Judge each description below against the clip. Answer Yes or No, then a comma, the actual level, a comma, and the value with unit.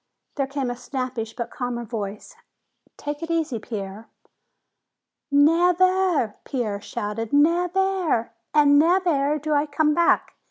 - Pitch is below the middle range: No, very high, 285 Hz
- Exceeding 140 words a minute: No, slow, 135 wpm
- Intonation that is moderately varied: No, wide, 5.9 semitones